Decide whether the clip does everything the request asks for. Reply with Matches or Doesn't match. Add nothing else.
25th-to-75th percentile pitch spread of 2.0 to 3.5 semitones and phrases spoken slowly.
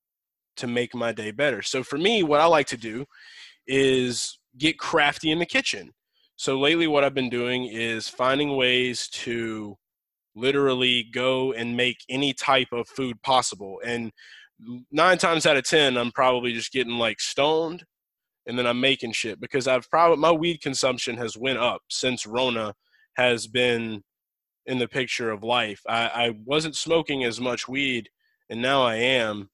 Doesn't match